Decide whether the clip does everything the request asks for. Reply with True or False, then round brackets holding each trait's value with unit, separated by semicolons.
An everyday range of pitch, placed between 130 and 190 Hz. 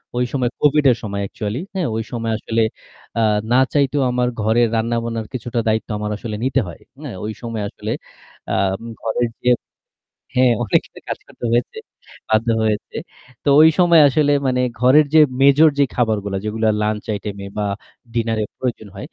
False (3.1 semitones; 115 Hz)